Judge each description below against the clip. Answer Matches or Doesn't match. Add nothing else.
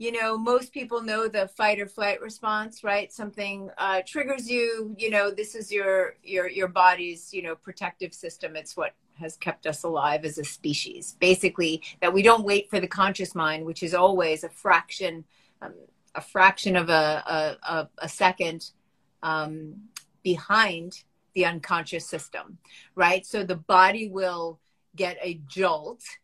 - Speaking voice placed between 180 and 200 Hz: Matches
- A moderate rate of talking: Matches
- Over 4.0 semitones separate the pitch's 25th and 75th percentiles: Doesn't match